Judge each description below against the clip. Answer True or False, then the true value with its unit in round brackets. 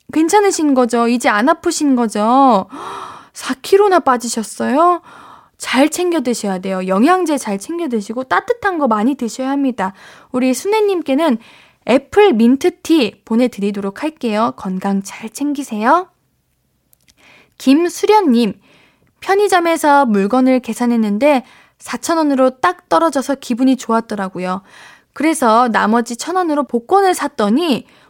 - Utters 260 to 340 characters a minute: True (275 characters per minute)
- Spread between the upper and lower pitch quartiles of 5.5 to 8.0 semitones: True (6.1 semitones)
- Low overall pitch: False (260 Hz)